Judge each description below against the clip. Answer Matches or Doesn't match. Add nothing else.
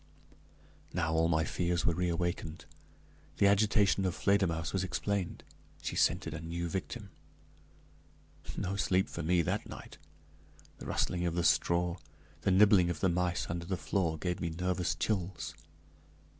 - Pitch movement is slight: Matches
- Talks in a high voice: Doesn't match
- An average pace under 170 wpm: Matches